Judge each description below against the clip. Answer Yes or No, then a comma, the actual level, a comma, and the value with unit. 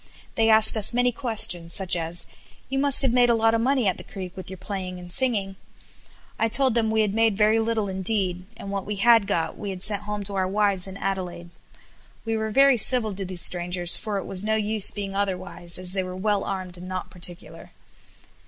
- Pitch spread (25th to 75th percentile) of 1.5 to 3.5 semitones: Yes, average, 3.2 semitones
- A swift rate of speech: Yes, fast, 220 wpm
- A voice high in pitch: Yes, high, 200 Hz